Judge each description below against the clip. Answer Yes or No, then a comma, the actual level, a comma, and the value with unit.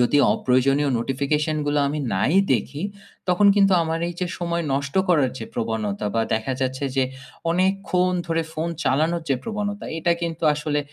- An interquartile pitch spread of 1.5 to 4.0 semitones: No, average, 4.5 semitones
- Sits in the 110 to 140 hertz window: No, medium, 150 Hz